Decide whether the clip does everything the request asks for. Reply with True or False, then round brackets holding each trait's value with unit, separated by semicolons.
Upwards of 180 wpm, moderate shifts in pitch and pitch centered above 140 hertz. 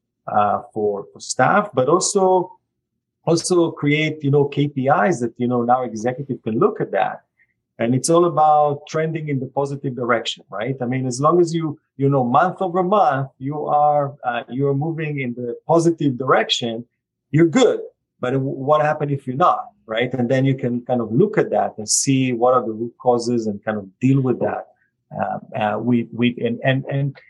False (195 wpm; 3.9 semitones; 135 Hz)